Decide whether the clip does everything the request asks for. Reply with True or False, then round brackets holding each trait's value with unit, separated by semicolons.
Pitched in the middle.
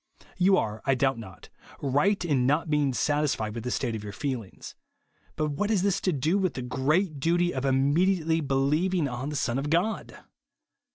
True (145 Hz)